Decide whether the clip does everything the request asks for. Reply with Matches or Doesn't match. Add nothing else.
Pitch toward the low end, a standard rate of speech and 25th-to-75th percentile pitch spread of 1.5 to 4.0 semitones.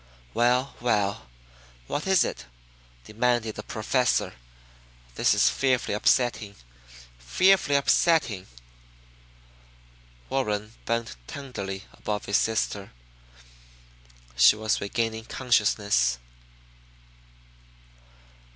Doesn't match